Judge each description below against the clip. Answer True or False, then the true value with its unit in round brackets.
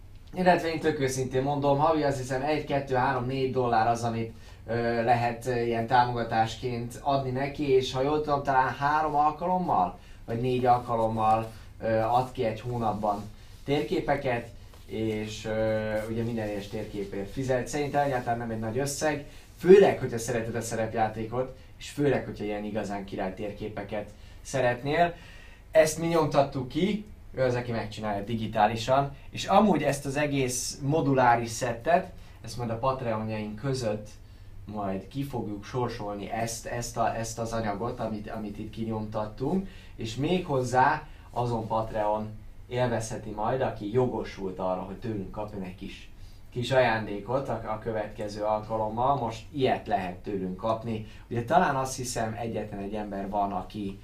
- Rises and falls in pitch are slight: False (3.6 semitones)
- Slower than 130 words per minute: False (150 wpm)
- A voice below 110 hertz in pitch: False (115 Hz)